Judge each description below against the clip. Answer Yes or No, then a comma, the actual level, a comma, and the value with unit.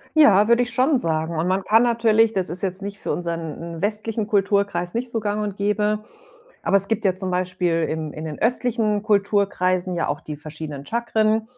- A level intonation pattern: No, average, 3.9 semitones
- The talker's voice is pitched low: No, high, 200 Hz